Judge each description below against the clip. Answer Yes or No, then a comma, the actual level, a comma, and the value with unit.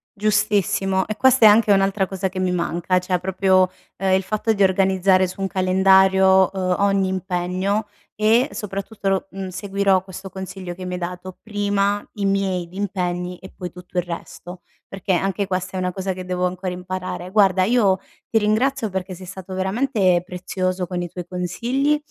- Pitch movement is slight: Yes, narrow, 1.5 semitones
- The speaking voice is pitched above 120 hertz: Yes, high, 190 Hz